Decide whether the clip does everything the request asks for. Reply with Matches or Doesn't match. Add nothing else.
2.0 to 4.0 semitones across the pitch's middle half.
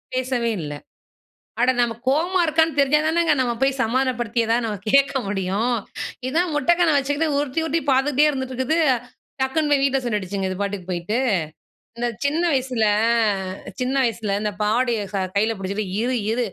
Doesn't match